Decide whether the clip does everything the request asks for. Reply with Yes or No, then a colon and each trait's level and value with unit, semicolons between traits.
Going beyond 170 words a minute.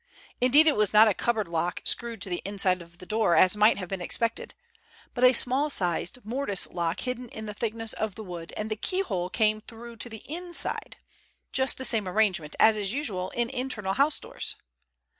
Yes: average, 200 wpm